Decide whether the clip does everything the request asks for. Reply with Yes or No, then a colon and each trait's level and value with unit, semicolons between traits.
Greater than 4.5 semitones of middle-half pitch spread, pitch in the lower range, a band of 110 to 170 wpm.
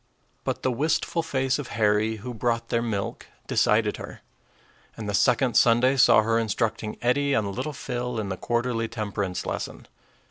No: average, 2.7 semitones; low, 115 Hz; average, 165 wpm